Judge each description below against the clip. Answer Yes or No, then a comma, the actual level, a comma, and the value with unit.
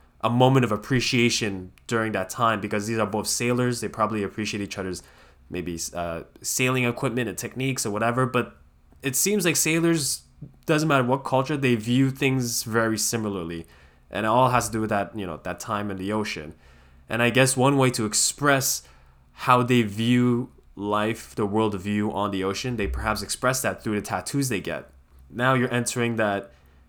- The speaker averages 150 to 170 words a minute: No, average, 185 wpm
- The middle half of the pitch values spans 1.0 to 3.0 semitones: No, average, 4.5 semitones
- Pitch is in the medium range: No, low, 110 Hz